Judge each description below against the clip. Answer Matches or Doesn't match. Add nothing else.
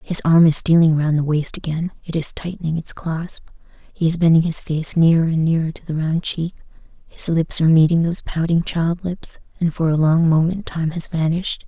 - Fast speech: Matches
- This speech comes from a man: Doesn't match